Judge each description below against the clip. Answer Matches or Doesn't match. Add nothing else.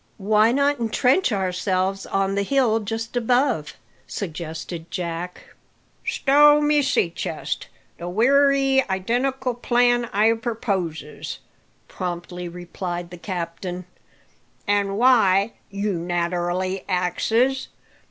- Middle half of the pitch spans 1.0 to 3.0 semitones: Doesn't match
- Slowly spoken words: Matches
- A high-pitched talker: Matches